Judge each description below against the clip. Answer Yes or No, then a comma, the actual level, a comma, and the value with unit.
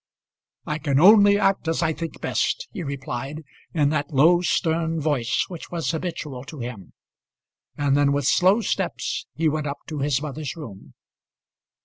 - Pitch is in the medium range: Yes, medium, 155 Hz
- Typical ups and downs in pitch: Yes, average, 3.0 semitones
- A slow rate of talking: No, average, 160 wpm